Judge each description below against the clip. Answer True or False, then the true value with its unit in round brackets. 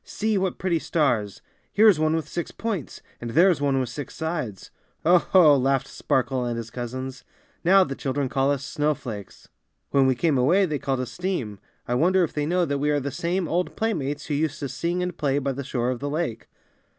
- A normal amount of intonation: True (4.7 semitones)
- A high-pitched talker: False (145 Hz)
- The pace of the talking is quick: True (225 wpm)